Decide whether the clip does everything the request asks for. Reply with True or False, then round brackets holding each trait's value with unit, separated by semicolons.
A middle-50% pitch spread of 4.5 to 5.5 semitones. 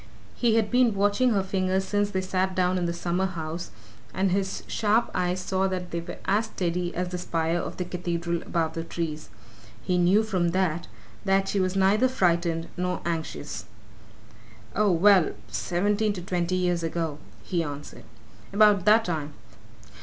False (2.4 semitones)